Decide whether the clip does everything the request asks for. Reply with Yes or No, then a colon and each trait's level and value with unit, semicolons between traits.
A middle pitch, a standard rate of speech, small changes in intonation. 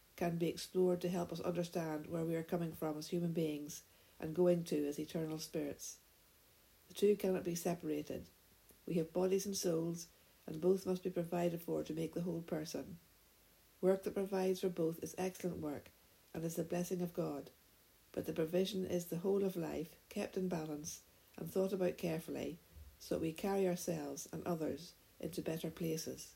Yes: medium, 170 Hz; average, 185 wpm; narrow, 2.3 semitones